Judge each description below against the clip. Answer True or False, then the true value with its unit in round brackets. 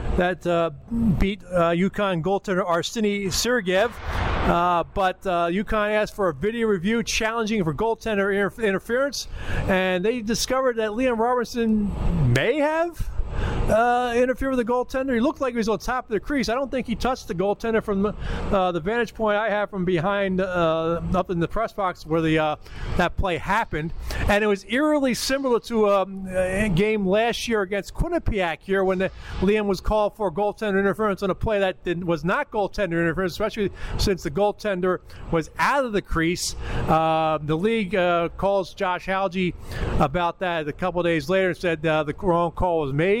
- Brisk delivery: False (185 wpm)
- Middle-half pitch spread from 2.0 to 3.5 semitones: False (4.0 semitones)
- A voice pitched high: True (195 Hz)